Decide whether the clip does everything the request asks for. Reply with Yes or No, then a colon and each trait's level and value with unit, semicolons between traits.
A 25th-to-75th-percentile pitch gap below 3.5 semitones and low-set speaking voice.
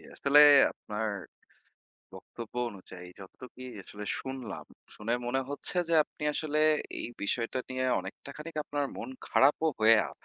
No: average, 5.2 semitones; low, 125 Hz